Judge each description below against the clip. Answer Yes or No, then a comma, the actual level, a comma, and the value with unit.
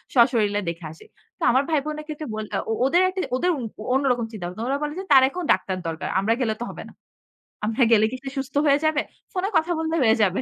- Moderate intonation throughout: No, wide, 5.9 semitones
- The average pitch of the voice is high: Yes, very high, 260 Hz